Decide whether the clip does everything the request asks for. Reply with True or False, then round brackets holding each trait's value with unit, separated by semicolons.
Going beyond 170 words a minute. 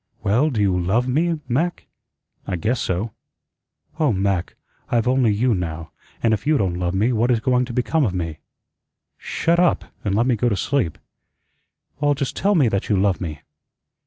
True (190 wpm)